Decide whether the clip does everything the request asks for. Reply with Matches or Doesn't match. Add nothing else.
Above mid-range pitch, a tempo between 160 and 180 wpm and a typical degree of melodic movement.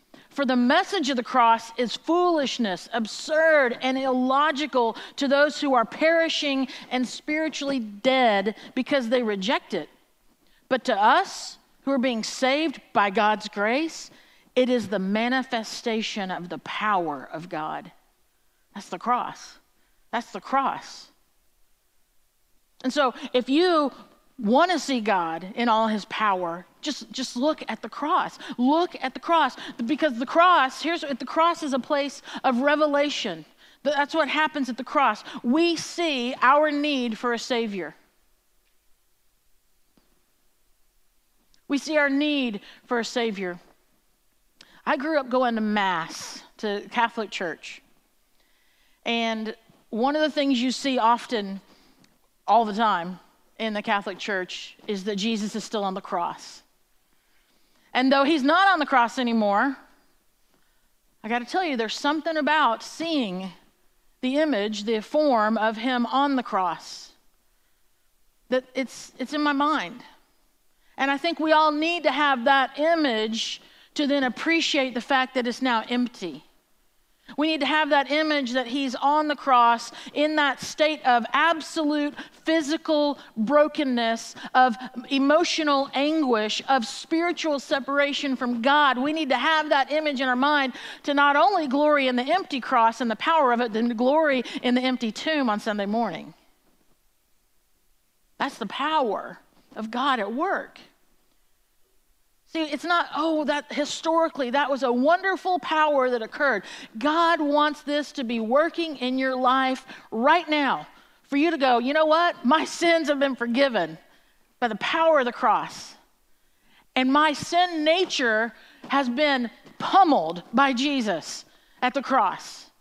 Doesn't match